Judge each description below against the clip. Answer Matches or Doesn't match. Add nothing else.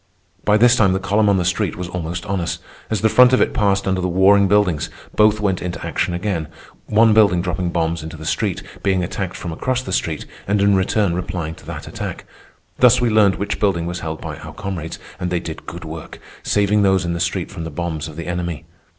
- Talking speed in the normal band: Doesn't match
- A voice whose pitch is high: Doesn't match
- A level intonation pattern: Doesn't match